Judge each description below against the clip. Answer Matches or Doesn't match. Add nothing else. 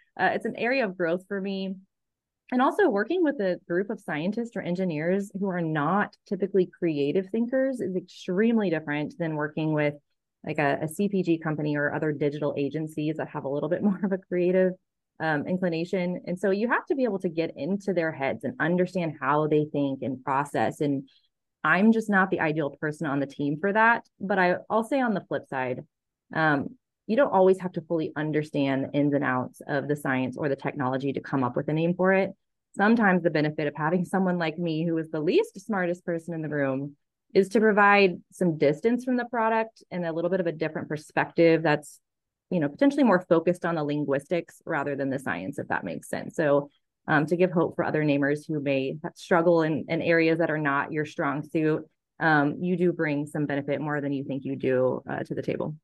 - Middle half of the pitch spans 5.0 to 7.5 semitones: Doesn't match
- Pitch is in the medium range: Matches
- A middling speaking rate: Doesn't match